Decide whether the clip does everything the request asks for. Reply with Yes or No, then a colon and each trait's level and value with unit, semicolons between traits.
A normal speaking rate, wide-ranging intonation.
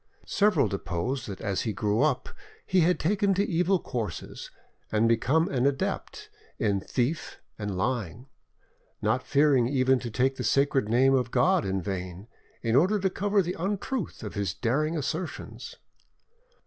Yes: average, 155 wpm; wide, 7.8 semitones